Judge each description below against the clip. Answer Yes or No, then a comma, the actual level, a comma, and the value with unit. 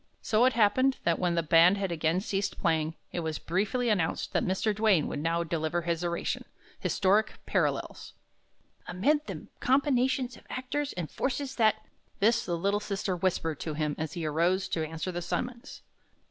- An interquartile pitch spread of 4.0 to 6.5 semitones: Yes, average, 5.2 semitones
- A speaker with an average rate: Yes, average, 175 wpm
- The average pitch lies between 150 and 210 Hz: Yes, medium, 185 Hz